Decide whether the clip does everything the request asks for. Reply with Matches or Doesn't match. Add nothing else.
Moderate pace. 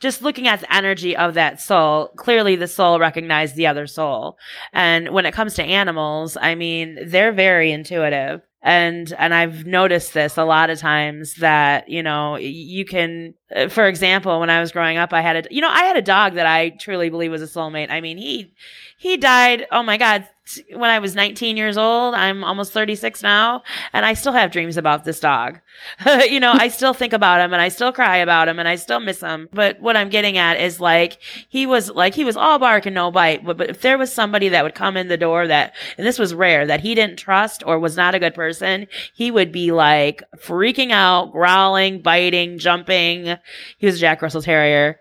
Doesn't match